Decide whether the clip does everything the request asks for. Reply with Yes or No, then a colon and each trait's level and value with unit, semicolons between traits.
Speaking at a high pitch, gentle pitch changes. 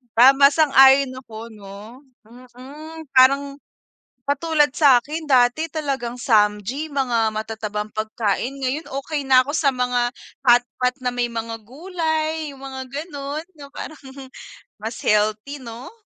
No: very high, 265 Hz; average, 3.8 semitones